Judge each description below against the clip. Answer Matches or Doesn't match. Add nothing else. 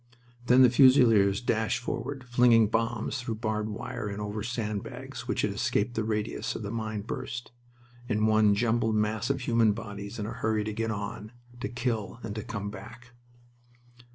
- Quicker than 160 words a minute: Matches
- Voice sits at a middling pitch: Doesn't match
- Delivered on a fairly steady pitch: Matches